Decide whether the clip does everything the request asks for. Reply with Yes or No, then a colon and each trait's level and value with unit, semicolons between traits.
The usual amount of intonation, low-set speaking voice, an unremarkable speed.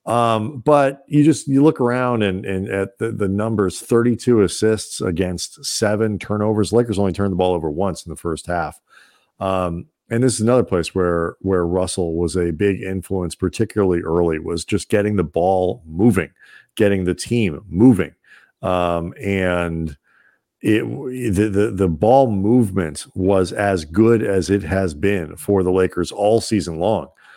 Yes: average, 3.6 semitones; low, 100 Hz; average, 165 wpm